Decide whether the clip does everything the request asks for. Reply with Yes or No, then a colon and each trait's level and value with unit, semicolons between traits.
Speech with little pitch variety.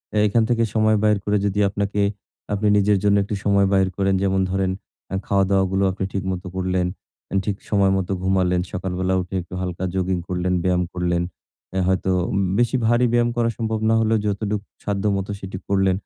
Yes: narrow, 1.8 semitones